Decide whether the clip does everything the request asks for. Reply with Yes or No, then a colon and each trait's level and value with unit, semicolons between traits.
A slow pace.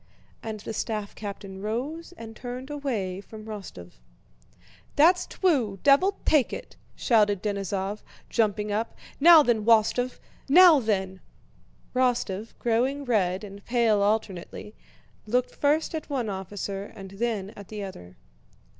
Yes: slow, 130 wpm